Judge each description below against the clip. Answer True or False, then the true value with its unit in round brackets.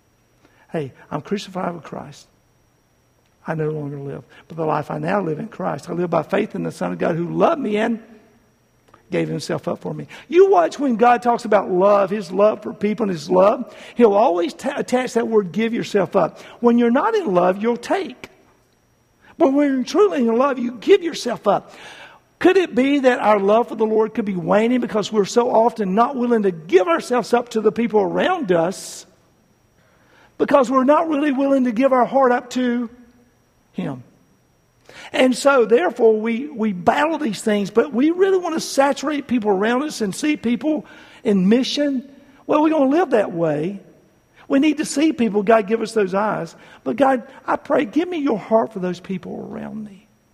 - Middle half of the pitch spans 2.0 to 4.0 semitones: False (5.4 semitones)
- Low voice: False (230 Hz)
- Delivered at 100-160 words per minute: False (200 wpm)